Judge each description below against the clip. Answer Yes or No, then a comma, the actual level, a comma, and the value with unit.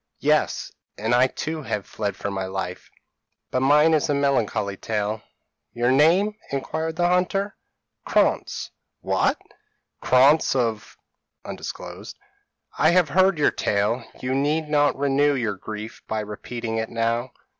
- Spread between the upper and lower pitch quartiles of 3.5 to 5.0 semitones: No, wide, 5.6 semitones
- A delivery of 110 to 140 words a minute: Yes, slow, 135 wpm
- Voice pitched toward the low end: Yes, low, 130 Hz